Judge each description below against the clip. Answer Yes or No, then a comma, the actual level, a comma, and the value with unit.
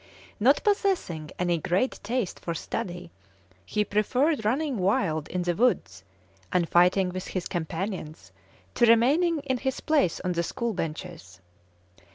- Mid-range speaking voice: No, high, 195 Hz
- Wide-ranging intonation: Yes, wide, 6.7 semitones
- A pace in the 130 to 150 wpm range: Yes, average, 140 wpm